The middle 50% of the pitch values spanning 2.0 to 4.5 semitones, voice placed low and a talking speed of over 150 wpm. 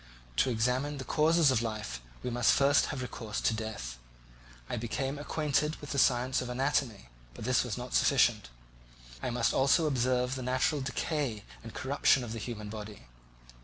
Yes: average, 3.6 semitones; low, 125 Hz; average, 170 wpm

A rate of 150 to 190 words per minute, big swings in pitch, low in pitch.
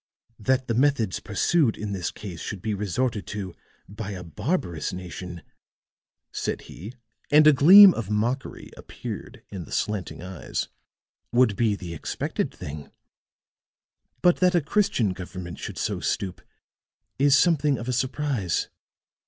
No: average, 140 wpm; wide, 6.7 semitones; low, 105 Hz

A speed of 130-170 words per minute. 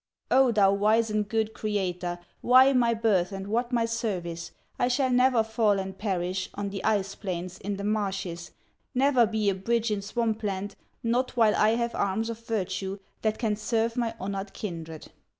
No: average, 180 wpm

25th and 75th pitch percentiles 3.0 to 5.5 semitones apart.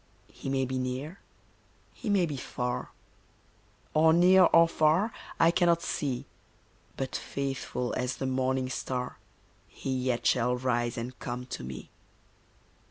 Yes: average, 4.5 semitones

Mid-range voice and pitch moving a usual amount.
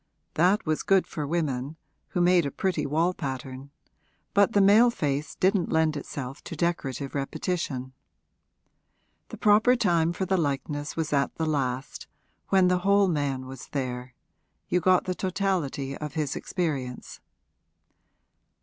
Yes: medium, 155 Hz; average, 4.9 semitones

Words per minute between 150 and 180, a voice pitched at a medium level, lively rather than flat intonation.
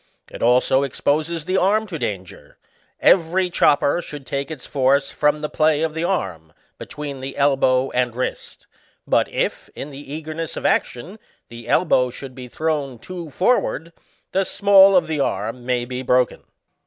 No: average, 170 wpm; medium, 145 Hz; average, 4.4 semitones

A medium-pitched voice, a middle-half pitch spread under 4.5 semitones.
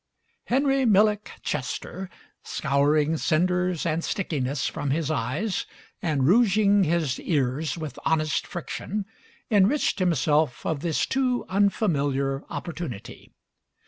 No: medium, 165 Hz; wide, 5.5 semitones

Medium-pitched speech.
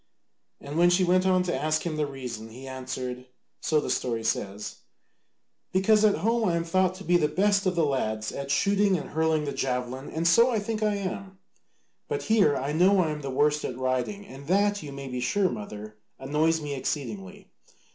Yes: medium, 155 Hz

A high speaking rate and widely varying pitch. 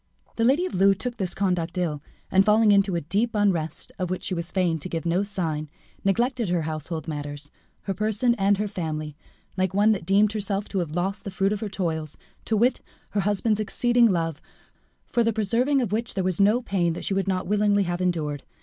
No: fast, 215 wpm; average, 3.6 semitones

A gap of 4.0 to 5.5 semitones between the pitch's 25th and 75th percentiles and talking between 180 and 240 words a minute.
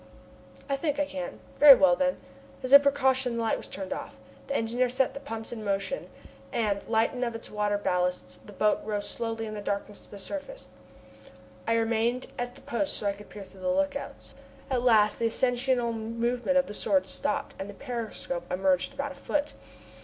Yes: average, 4.7 semitones; average, 200 wpm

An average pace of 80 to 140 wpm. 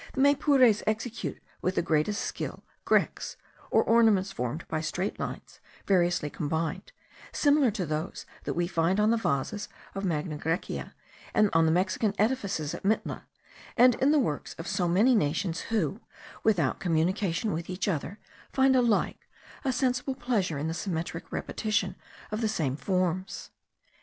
No: average, 150 wpm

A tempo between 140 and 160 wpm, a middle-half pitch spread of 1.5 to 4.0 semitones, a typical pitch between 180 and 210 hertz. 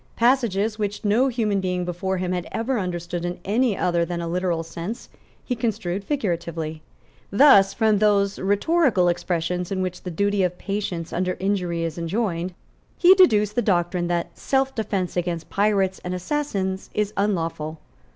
Yes: average, 155 wpm; average, 3.3 semitones; high, 190 Hz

